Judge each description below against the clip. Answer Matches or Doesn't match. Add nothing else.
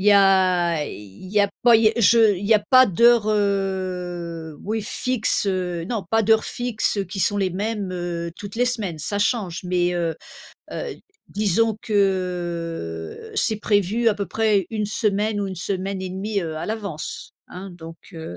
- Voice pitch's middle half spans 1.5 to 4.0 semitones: Matches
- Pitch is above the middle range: Matches